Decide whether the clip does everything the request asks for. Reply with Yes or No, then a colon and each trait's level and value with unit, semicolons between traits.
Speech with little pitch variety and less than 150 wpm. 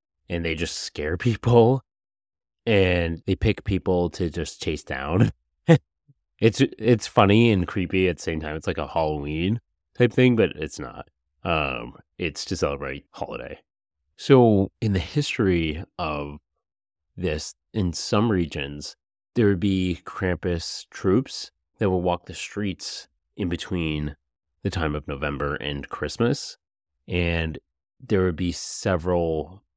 No: average, 4.7 semitones; slow, 135 wpm